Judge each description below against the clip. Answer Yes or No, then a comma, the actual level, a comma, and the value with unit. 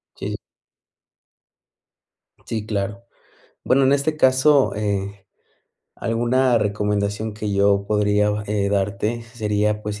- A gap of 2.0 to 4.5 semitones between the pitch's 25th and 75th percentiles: Yes, narrow, 2.4 semitones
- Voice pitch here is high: No, low, 105 Hz